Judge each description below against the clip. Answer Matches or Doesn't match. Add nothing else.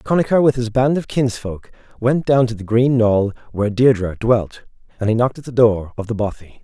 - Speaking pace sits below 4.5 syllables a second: Doesn't match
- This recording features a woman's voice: Doesn't match